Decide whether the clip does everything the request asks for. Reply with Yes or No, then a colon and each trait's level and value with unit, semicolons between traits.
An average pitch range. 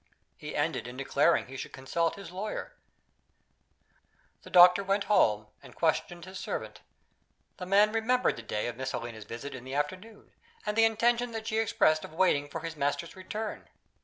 No: wide, 7.4 semitones